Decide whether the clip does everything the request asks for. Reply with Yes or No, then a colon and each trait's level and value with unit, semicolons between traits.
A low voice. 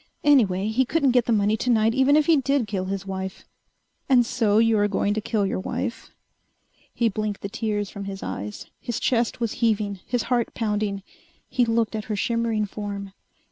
No: high, 220 Hz